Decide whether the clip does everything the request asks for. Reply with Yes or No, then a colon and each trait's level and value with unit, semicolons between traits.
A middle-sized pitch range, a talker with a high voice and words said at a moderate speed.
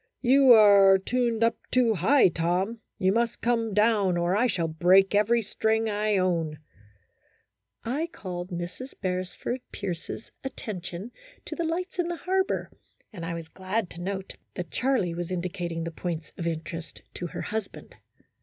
Yes: average, 4.9 semitones; high, 195 Hz; average, 160 wpm